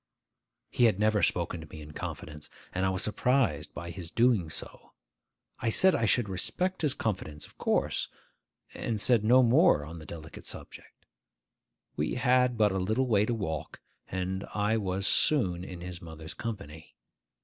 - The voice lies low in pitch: Yes, low, 100 Hz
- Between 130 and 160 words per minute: No, average, 170 wpm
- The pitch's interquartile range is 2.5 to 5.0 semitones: No, wide, 5.6 semitones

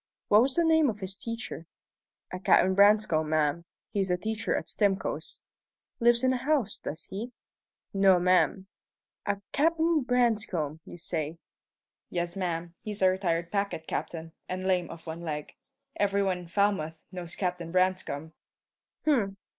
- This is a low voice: No, high, 190 Hz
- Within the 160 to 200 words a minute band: No, average, 150 wpm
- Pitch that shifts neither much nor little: Yes, average, 4.0 semitones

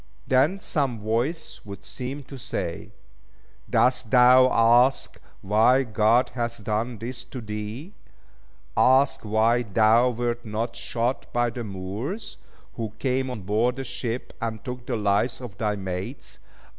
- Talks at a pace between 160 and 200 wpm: No, average, 140 wpm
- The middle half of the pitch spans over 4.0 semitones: No, average, 2.9 semitones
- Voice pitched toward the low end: Yes, low, 120 Hz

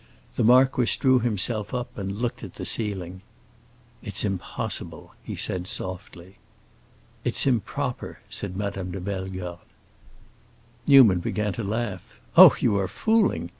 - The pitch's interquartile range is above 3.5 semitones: Yes, average, 4.4 semitones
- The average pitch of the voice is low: Yes, low, 100 Hz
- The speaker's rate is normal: No, slow, 130 wpm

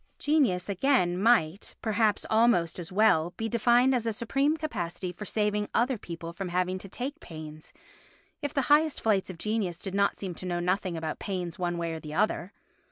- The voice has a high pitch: Yes, high, 195 Hz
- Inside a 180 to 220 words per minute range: Yes, average, 190 wpm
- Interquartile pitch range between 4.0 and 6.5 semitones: Yes, average, 5.0 semitones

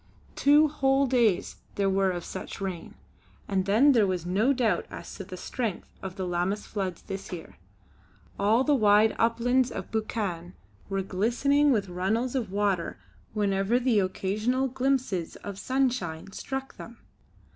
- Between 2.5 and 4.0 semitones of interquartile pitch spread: No, average, 4.9 semitones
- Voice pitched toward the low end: No, high, 210 Hz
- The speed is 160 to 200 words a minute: No, average, 150 wpm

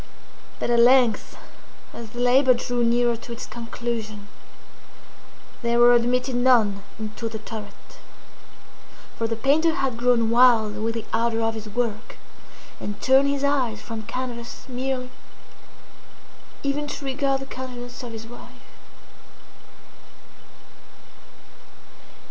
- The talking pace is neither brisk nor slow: No, slow, 120 wpm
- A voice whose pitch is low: No, high, 240 Hz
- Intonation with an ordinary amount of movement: No, narrow, 2.2 semitones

